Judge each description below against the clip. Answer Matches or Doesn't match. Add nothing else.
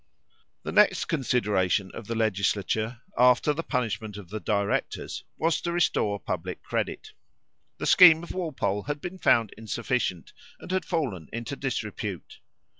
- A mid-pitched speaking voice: Doesn't match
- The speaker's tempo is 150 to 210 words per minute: Doesn't match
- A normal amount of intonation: Doesn't match